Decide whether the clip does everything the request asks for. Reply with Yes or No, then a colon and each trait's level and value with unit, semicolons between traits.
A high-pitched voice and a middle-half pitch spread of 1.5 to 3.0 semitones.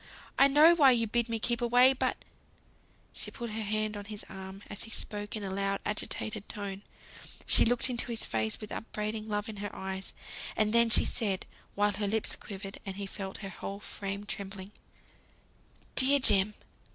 Yes: high, 210 Hz; narrow, 2.6 semitones